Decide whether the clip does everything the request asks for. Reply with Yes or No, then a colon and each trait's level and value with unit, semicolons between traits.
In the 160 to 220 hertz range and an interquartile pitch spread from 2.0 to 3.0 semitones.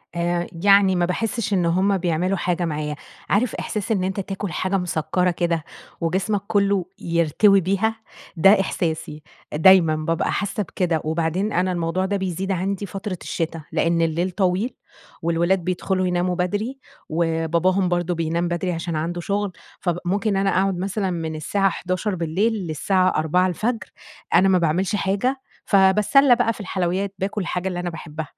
Yes: medium, 185 Hz; average, 2.7 semitones